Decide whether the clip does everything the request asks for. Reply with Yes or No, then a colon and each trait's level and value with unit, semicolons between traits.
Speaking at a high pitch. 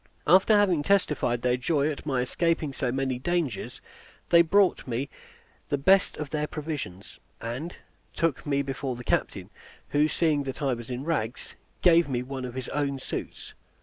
No: medium, 140 Hz